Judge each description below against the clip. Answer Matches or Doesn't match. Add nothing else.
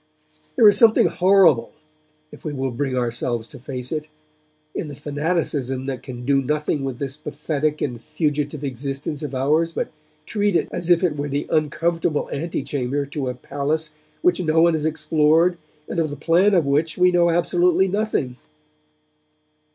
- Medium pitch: Matches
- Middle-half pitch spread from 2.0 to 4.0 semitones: Matches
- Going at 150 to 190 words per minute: Matches